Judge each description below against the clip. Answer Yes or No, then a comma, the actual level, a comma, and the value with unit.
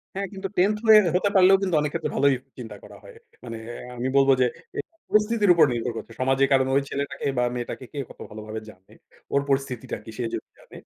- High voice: No, medium, 140 Hz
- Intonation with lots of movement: Yes, wide, 7.6 semitones